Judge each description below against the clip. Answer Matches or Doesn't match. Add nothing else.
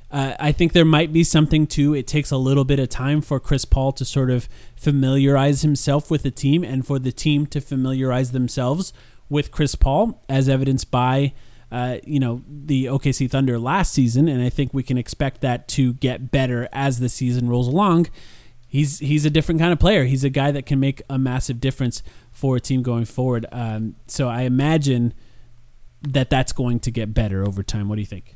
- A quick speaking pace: Matches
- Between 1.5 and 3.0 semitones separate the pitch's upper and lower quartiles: Matches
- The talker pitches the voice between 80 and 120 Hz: Doesn't match